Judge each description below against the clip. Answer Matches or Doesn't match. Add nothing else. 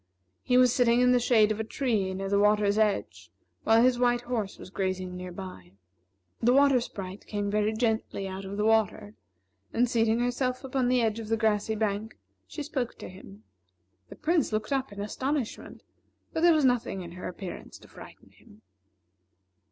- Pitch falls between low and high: Doesn't match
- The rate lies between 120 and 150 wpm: Doesn't match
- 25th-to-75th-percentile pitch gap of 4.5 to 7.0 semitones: Doesn't match